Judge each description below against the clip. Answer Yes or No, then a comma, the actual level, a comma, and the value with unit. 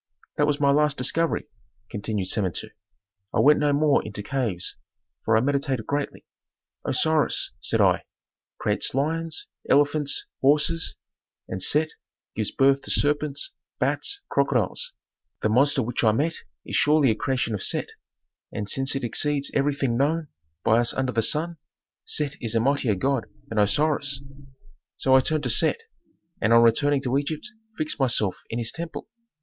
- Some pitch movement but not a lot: Yes, average, 4.2 semitones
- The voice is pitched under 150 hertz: Yes, medium, 140 Hz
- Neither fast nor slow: Yes, average, 155 wpm